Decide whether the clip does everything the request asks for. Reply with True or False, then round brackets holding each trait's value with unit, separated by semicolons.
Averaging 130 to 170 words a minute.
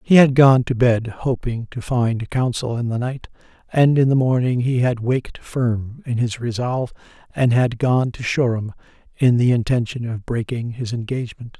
False (180 wpm)